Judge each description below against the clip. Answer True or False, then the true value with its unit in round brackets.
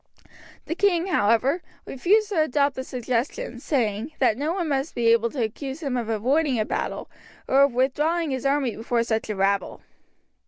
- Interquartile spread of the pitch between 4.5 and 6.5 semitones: True (5.1 semitones)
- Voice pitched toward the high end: True (265 Hz)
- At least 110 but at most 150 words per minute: False (180 wpm)